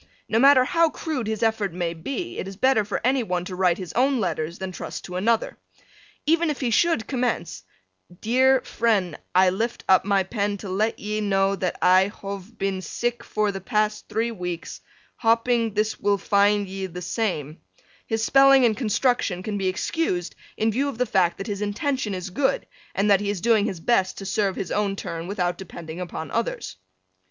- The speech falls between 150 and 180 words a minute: No, average, 195 wpm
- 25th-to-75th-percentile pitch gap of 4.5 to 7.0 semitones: No, average, 3.8 semitones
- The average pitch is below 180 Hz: No, high, 205 Hz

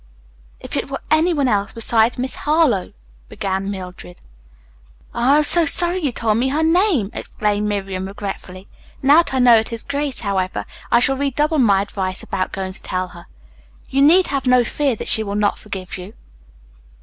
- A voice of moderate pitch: No, high, 230 Hz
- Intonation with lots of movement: Yes, wide, 6.3 semitones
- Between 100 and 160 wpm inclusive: No, average, 185 wpm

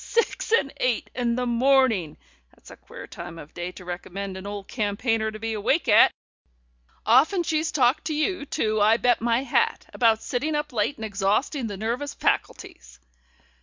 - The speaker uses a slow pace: No, average, 175 wpm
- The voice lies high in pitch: Yes, high, 230 Hz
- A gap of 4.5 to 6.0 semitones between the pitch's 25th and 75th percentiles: Yes, average, 5.0 semitones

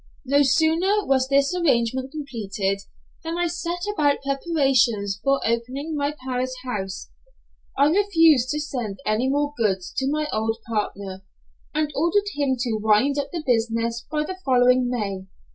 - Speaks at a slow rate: No, average, 150 wpm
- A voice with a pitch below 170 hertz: No, very high, 265 Hz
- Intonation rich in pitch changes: No, average, 4.7 semitones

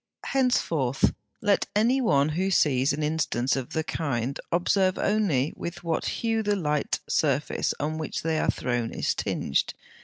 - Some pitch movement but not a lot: No, wide, 6.2 semitones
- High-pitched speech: No, medium, 160 Hz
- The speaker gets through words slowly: No, average, 155 wpm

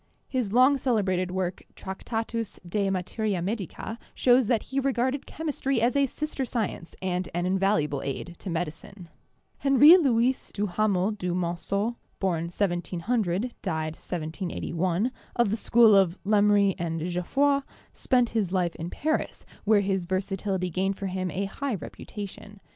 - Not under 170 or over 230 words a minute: No, average, 140 wpm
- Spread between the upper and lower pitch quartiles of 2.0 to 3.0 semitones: No, average, 4.8 semitones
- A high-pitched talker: Yes, high, 200 Hz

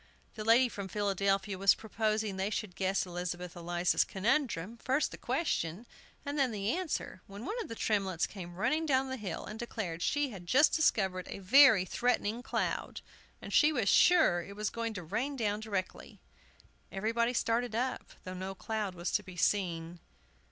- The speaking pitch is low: No, high, 210 Hz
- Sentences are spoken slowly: No, average, 175 wpm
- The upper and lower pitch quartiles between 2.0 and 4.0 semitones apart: No, average, 4.5 semitones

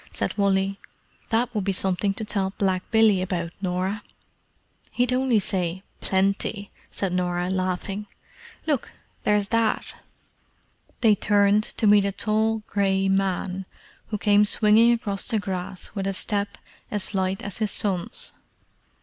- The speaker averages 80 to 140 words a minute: Yes, slow, 135 wpm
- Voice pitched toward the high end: Yes, high, 200 Hz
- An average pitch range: No, narrow, 2.0 semitones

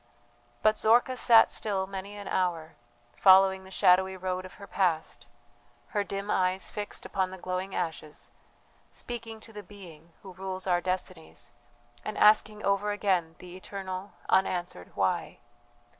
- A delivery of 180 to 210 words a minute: No, average, 145 wpm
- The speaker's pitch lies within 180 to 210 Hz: Yes, high, 190 Hz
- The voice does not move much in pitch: Yes, narrow, 2.1 semitones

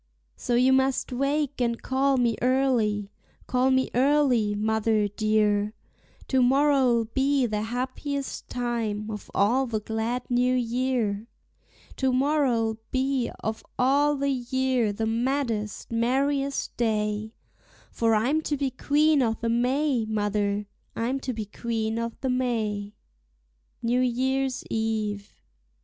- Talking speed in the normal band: No, slow, 125 wpm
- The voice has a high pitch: Yes, high, 245 Hz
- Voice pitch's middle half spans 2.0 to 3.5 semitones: Yes, average, 3.2 semitones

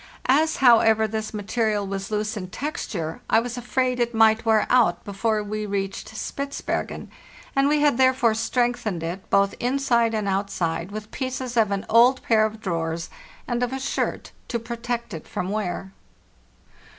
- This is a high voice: Yes, high, 220 Hz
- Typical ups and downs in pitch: Yes, average, 3.6 semitones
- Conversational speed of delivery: Yes, average, 160 wpm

